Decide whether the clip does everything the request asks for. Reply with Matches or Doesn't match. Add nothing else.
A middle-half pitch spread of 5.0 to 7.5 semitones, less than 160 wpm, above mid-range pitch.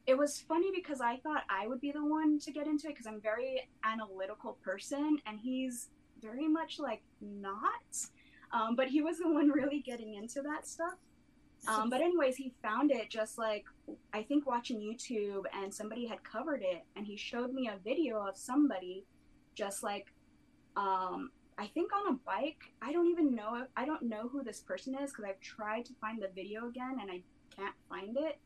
Doesn't match